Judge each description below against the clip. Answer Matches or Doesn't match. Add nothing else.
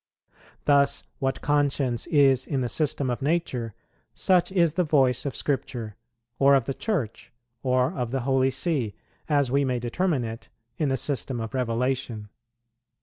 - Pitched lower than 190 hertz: Matches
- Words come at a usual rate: Matches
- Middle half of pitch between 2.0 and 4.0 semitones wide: Matches